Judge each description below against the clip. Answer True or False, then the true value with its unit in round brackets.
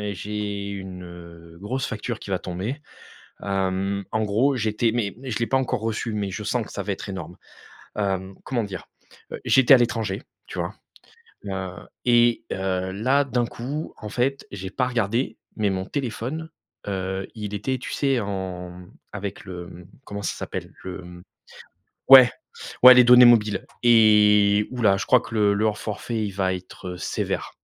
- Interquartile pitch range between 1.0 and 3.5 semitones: False (4.0 semitones)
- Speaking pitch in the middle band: False (105 Hz)